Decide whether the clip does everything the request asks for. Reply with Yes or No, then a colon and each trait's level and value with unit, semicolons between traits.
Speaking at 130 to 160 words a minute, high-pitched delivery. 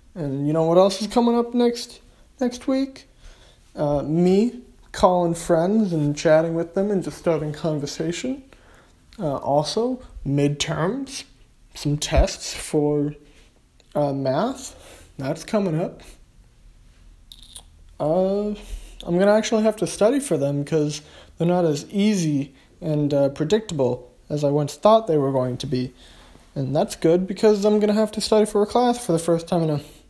No: average, 155 wpm; medium, 165 Hz